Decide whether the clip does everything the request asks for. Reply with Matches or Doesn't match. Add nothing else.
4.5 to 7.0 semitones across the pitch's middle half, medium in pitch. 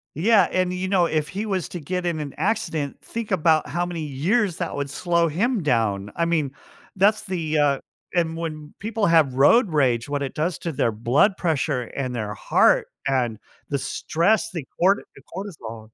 Matches